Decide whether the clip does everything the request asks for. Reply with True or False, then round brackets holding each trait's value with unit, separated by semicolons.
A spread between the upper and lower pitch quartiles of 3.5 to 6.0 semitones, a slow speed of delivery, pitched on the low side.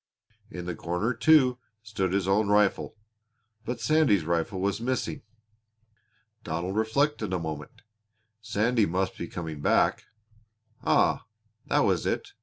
True (4.4 semitones; 125 wpm; 100 Hz)